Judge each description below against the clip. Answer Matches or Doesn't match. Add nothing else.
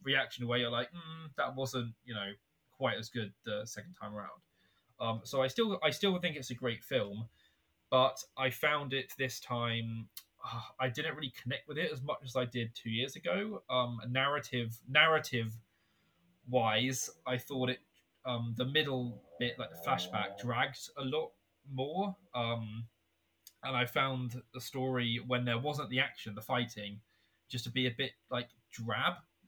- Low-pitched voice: Matches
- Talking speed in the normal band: Matches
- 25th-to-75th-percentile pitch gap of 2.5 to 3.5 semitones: Matches